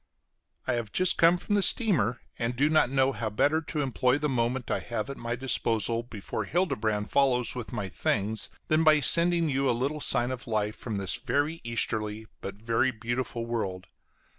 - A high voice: No, low, 120 Hz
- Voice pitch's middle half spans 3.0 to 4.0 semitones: No, average, 4.6 semitones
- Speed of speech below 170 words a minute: No, average, 190 wpm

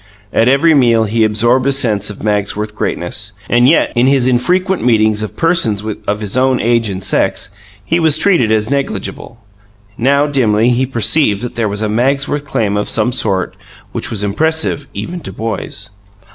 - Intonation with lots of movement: No, average, 4.5 semitones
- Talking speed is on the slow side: No, average, 175 wpm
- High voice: No, low, 120 Hz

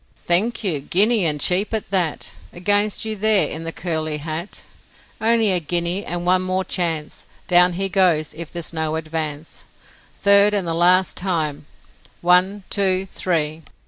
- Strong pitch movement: No, average, 3.3 semitones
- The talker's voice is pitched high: No, medium, 180 Hz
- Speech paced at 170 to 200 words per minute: No, average, 155 wpm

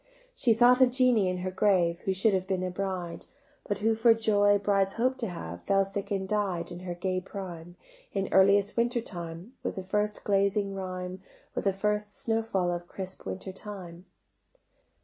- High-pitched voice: Yes, high, 195 Hz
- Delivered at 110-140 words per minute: No, average, 190 wpm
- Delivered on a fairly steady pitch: Yes, narrow, 2.3 semitones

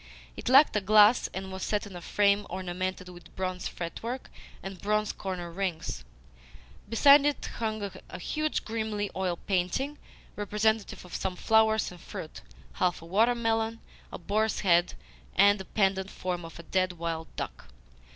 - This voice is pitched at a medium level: No, high, 195 Hz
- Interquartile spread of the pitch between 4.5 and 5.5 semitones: No, average, 3.3 semitones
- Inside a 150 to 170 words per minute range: Yes, average, 160 wpm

